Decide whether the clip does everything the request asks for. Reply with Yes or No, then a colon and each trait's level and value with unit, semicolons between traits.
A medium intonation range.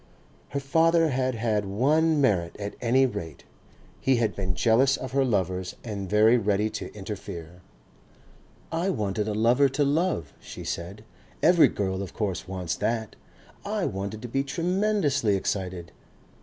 No: wide, 6.0 semitones